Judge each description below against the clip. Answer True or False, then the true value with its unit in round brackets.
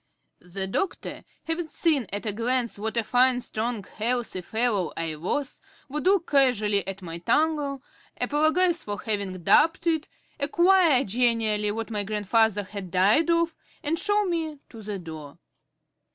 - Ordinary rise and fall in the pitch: False (7.1 semitones)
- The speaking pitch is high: True (235 Hz)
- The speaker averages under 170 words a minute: True (150 wpm)